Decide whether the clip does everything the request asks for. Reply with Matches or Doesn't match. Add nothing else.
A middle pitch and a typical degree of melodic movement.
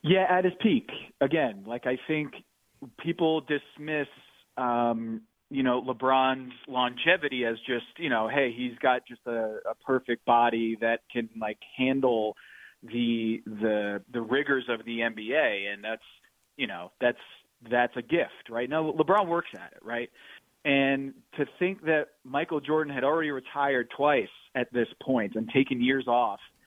Doesn't match